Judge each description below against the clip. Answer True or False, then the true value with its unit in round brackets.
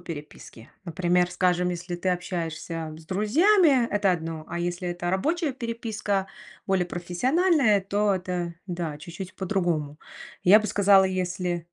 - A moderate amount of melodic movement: True (3.0 semitones)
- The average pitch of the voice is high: False (180 Hz)